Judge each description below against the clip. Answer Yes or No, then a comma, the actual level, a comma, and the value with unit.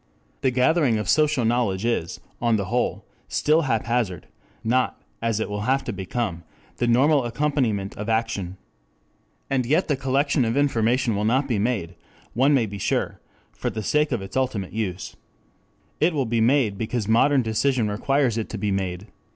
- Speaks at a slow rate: No, average, 175 wpm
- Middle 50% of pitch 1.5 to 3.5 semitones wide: No, average, 4.1 semitones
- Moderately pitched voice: No, low, 115 Hz